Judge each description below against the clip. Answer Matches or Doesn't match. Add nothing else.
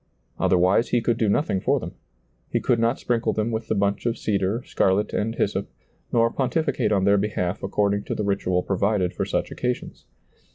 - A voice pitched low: Matches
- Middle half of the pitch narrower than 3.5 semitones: Matches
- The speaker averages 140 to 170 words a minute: Doesn't match